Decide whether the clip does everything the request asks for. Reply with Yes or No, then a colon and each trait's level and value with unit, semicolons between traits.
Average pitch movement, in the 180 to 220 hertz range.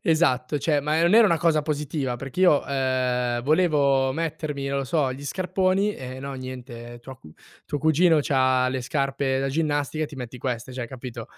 No: average, 3.3 semitones; low, 135 Hz